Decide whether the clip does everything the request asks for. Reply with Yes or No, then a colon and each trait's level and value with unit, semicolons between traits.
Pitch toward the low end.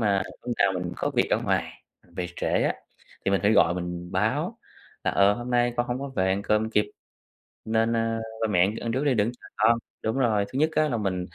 Yes: low, 110 Hz